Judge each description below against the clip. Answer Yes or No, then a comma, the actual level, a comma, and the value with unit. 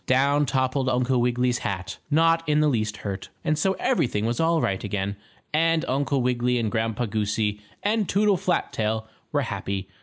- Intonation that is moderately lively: No, wide, 5.9 semitones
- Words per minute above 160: Yes, average, 175 wpm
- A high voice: No, low, 125 Hz